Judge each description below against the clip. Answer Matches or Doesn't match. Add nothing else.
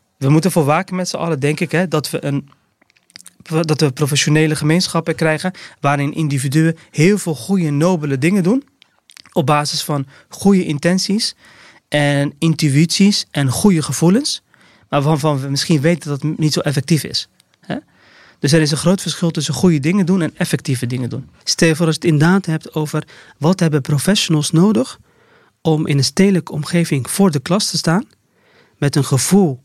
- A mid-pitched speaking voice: Matches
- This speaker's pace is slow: Doesn't match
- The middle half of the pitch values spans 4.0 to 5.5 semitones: Doesn't match